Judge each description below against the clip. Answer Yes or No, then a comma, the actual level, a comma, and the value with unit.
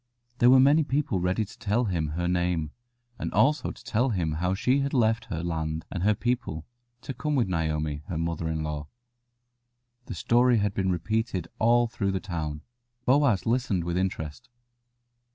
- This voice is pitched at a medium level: No, very low, 95 Hz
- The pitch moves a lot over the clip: Yes, wide, 6.6 semitones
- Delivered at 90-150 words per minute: No, average, 175 wpm